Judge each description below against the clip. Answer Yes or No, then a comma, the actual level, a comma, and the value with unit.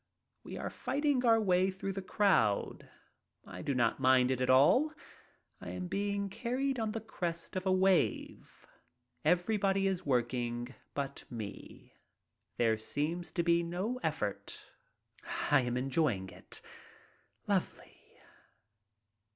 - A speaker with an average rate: No, slow, 130 wpm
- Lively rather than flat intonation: Yes, wide, 7.6 semitones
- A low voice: No, medium, 175 Hz